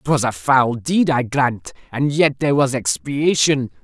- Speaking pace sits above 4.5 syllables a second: No, 4.1 syllables/s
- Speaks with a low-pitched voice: Yes, low, 130 Hz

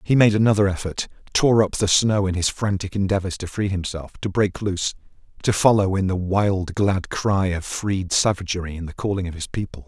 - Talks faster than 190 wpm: Yes, fast, 205 wpm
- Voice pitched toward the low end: Yes, very low, 95 Hz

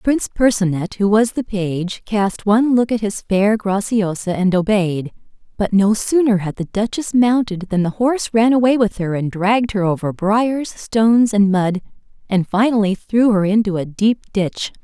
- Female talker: Yes, female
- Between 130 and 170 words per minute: No, average, 180 wpm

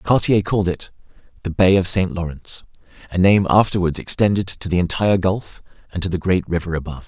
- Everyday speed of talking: Yes, average, 180 wpm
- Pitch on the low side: Yes, very low, 90 Hz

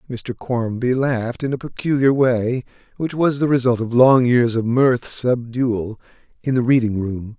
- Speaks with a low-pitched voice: Yes, low, 125 Hz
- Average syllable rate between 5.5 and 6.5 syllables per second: No, 4.4 syllables/s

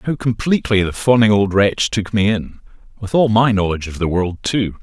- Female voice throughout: No, male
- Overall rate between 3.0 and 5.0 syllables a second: No, 5.3 syllables/s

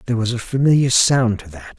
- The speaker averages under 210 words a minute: No, fast, 235 wpm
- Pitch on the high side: No, low, 115 Hz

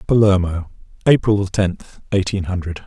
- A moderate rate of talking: No, slow, 105 wpm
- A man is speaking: Yes, male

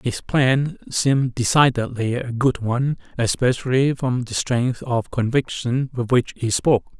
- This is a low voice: Yes, low, 125 Hz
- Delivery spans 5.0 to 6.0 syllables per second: No, 4.3 syllables/s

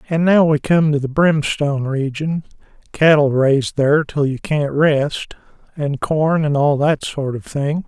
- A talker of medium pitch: Yes, medium, 145 Hz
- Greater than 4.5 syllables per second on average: No, 4.3 syllables/s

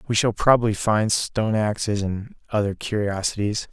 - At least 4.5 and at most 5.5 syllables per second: Yes, 5.0 syllables/s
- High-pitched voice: No, low, 105 Hz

